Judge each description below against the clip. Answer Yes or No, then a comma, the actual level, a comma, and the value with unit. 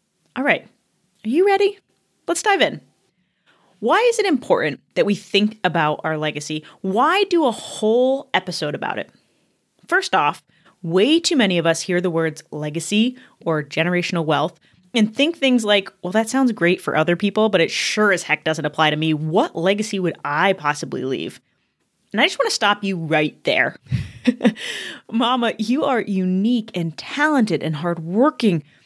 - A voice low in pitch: No, high, 200 Hz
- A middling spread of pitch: No, wide, 7.1 semitones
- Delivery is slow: No, average, 170 wpm